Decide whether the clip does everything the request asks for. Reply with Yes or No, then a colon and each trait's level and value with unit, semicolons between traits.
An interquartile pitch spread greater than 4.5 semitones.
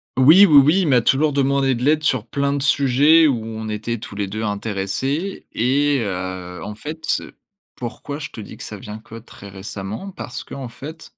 Yes: wide, 5.4 semitones